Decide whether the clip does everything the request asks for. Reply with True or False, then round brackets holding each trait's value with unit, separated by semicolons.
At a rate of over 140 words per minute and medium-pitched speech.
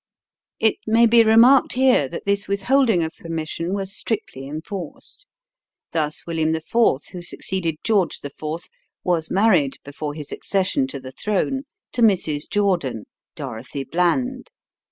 False (135 wpm; 180 Hz)